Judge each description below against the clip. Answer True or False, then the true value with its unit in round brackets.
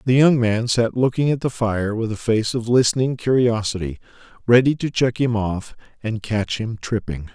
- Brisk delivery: False (190 wpm)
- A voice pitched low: True (115 Hz)